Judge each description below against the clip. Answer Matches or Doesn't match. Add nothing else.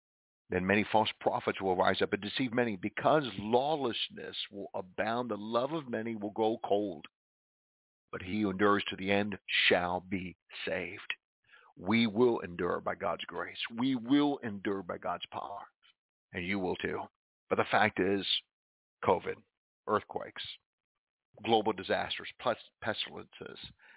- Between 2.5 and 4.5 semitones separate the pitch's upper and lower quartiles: Matches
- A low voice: Matches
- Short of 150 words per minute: Matches